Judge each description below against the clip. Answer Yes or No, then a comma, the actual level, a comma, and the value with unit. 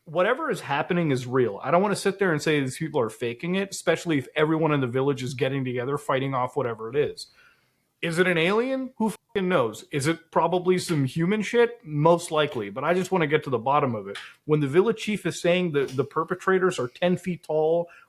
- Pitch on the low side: No, medium, 165 Hz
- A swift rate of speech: Yes, fast, 235 wpm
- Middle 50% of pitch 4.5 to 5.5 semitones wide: Yes, average, 4.8 semitones